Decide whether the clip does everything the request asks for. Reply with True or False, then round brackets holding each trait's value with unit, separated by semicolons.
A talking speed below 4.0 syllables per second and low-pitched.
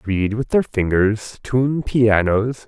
True (3.2 syllables/s; 115 Hz)